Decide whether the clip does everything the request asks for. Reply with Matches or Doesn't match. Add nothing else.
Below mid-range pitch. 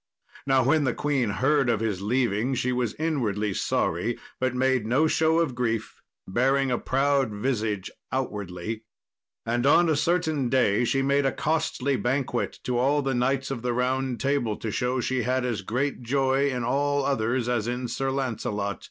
Matches